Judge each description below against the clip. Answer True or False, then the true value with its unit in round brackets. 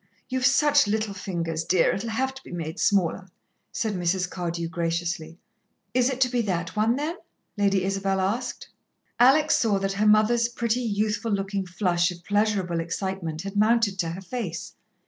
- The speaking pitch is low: False (195 Hz)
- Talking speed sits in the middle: True (165 wpm)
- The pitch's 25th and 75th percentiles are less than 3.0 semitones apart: False (4.6 semitones)